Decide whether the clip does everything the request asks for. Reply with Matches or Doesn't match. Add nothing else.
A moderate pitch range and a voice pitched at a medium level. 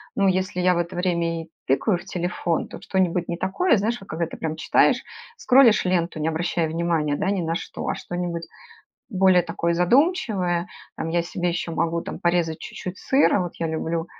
Doesn't match